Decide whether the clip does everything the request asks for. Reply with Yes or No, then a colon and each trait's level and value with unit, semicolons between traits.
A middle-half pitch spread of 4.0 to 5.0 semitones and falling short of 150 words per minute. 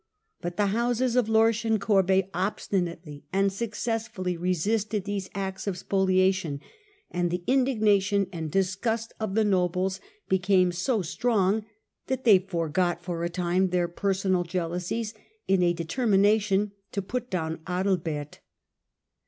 No: average, 3.2 semitones; slow, 135 wpm